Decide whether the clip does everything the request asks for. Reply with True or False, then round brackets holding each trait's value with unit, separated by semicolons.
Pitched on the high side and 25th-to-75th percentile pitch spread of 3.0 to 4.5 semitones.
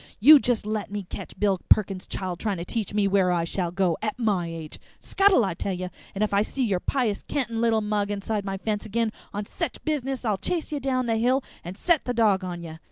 True (210 Hz; 3.9 semitones)